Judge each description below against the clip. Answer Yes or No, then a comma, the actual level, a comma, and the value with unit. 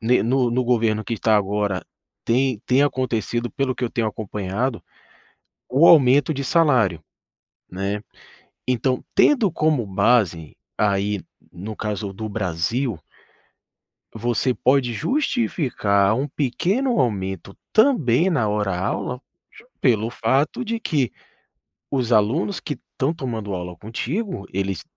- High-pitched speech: No, low, 120 Hz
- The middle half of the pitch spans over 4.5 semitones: Yes, average, 4.9 semitones